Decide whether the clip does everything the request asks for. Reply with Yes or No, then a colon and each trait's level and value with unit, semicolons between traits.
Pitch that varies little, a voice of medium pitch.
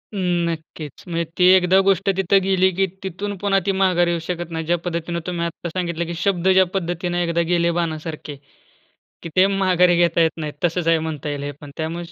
Yes: narrow, 2.0 semitones; medium, 175 Hz